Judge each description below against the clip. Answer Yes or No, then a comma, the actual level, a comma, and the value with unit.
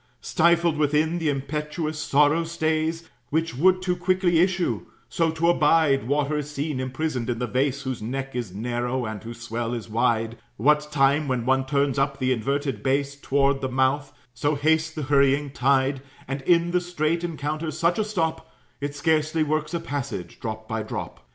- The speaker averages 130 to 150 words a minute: No, average, 175 wpm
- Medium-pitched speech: Yes, medium, 145 Hz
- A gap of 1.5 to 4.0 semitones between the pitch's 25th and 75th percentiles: Yes, average, 3.4 semitones